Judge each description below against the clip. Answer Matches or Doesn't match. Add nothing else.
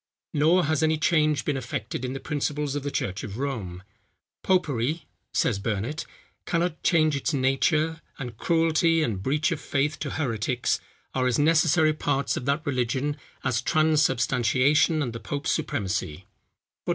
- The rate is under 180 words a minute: Matches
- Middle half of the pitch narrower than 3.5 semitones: Doesn't match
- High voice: Doesn't match